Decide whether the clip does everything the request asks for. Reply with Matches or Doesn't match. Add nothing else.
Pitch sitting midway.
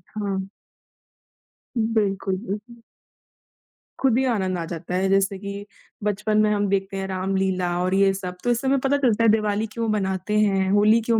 Doesn't match